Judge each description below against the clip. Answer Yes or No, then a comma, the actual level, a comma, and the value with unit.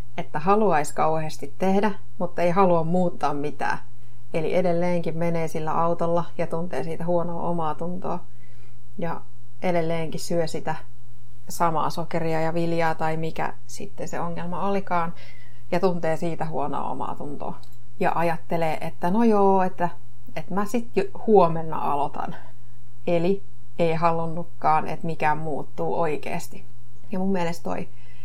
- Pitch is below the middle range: No, medium, 165 Hz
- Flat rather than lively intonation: No, average, 4.6 semitones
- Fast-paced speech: No, average, 135 wpm